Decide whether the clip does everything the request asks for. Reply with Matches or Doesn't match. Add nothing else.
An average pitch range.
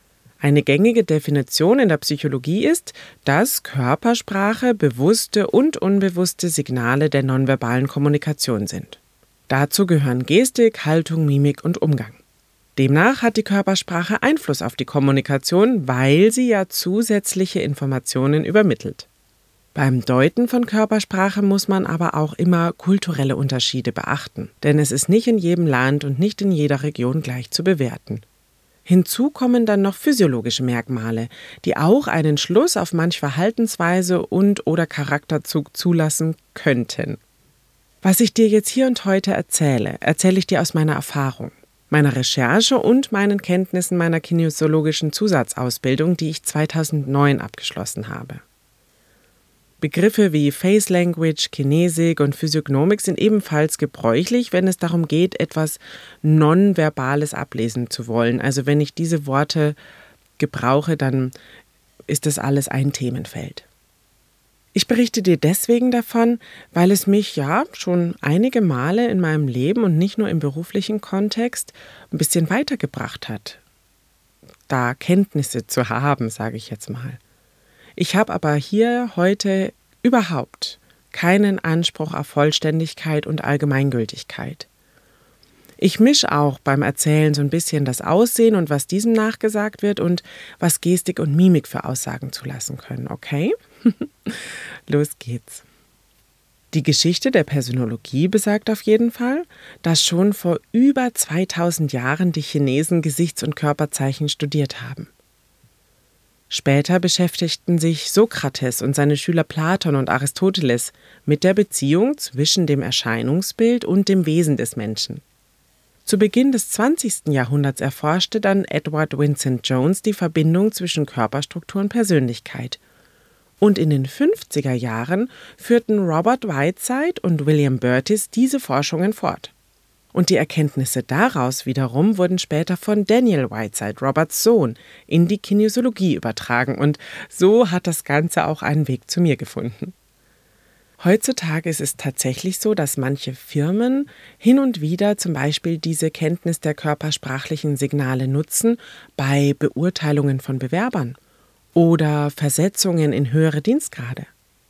Doesn't match